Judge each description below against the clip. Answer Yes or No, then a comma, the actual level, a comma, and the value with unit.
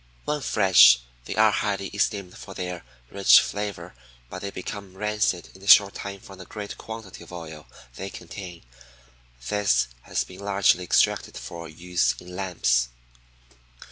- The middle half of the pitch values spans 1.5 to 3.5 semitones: Yes, narrow, 2.6 semitones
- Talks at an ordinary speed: Yes, average, 150 wpm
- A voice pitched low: Yes, very low, 95 Hz